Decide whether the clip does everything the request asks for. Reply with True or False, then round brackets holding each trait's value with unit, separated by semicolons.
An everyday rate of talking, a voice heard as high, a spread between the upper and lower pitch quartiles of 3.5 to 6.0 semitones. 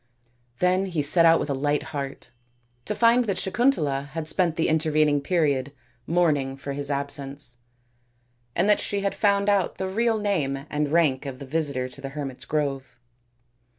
False (175 wpm; 150 Hz; 4.9 semitones)